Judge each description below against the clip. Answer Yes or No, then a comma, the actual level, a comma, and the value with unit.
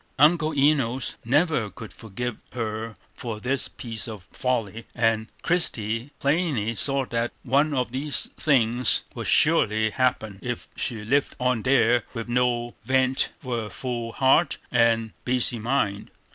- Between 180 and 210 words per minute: No, average, 140 wpm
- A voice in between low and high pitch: No, low, 120 Hz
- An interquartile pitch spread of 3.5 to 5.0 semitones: No, average, 2.9 semitones